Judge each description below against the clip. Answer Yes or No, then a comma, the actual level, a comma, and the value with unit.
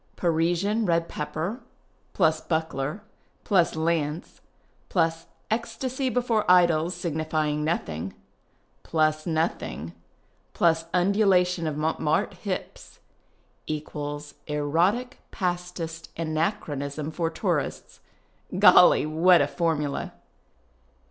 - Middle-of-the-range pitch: Yes, medium, 165 Hz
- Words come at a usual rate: No, slow, 90 wpm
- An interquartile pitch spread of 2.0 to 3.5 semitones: Yes, average, 2.8 semitones